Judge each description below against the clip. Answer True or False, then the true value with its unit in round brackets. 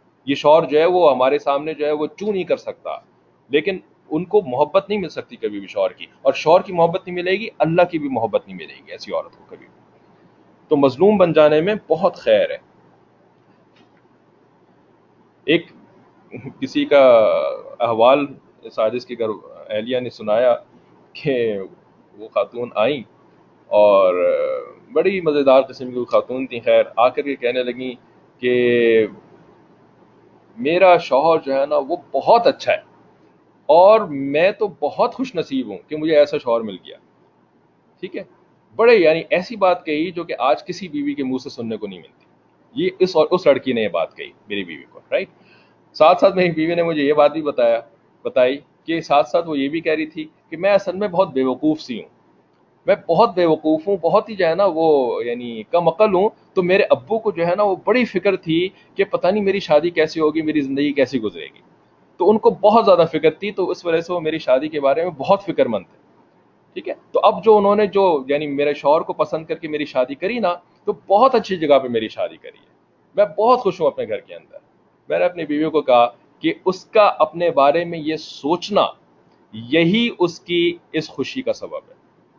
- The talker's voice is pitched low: False (165 Hz)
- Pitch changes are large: True (5.8 semitones)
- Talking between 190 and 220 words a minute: True (205 wpm)